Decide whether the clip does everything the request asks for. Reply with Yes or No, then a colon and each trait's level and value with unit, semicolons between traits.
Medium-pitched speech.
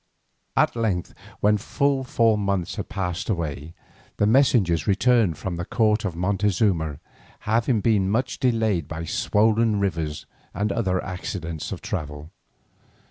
No: low, 100 Hz